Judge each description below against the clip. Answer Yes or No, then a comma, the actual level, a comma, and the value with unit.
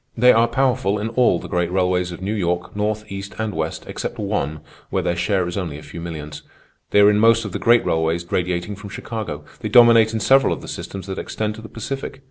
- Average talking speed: No, fast, 235 wpm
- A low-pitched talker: Yes, low, 100 Hz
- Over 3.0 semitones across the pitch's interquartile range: Yes, average, 4.2 semitones